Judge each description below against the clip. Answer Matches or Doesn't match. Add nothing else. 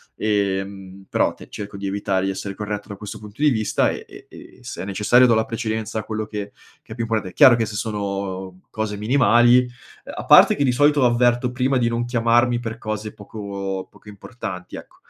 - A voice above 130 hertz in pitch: Doesn't match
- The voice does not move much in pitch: Doesn't match